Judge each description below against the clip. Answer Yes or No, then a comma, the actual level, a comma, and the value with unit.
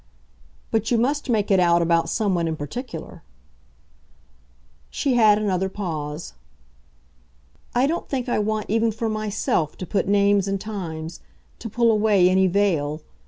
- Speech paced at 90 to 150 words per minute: Yes, average, 145 wpm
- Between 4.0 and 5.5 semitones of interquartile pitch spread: Yes, average, 4.4 semitones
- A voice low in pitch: No, high, 200 Hz